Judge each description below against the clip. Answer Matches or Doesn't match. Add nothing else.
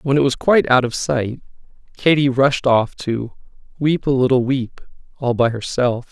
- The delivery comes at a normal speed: Matches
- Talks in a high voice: Doesn't match